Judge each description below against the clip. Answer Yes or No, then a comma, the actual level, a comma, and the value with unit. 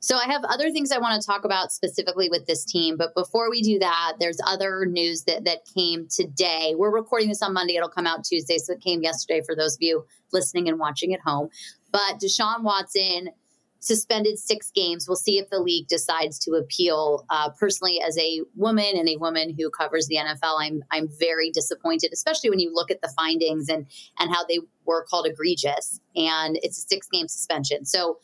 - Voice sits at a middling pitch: Yes, medium, 170 Hz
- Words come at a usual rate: No, fast, 210 wpm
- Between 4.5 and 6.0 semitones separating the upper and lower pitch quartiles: No, average, 3.5 semitones